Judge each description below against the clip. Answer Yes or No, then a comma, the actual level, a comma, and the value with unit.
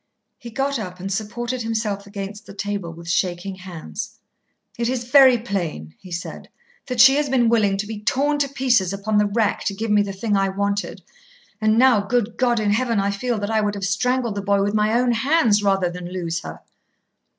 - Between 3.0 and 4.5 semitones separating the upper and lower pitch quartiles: Yes, average, 3.4 semitones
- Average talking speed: No, fast, 215 wpm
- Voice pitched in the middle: No, high, 210 Hz